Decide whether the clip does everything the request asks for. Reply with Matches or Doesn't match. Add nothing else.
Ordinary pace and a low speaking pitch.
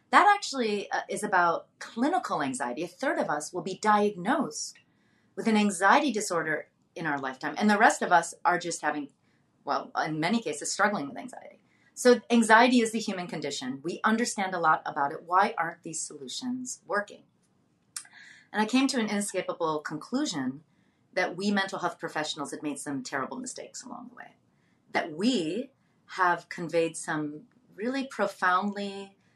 Doesn't match